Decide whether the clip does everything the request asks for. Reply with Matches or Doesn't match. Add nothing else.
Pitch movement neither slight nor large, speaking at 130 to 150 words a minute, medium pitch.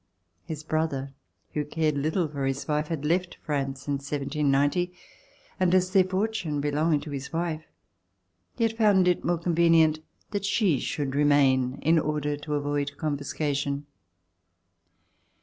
Matches